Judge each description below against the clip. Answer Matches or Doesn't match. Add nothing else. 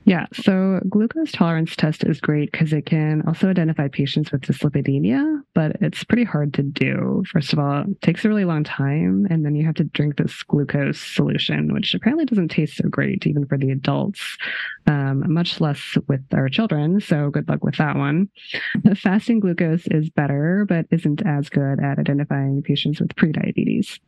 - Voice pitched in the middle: Matches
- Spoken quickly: Doesn't match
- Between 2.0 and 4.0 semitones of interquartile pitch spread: Doesn't match